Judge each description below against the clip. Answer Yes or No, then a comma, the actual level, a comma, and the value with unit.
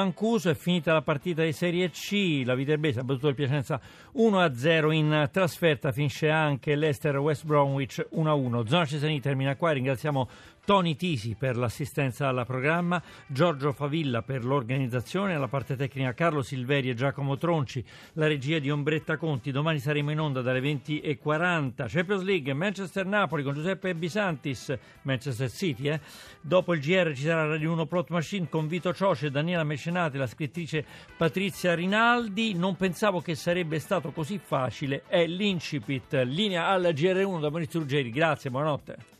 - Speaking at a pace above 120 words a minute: Yes, average, 155 wpm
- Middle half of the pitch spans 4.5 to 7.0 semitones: No, average, 3.9 semitones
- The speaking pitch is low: No, medium, 155 Hz